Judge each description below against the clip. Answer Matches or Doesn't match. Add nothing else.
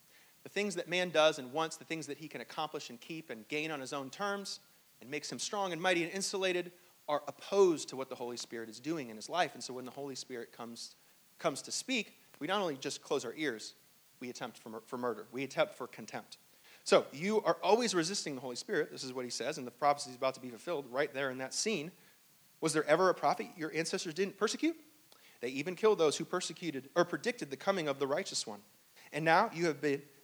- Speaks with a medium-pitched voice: Matches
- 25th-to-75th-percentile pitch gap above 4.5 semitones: Matches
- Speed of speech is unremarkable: Doesn't match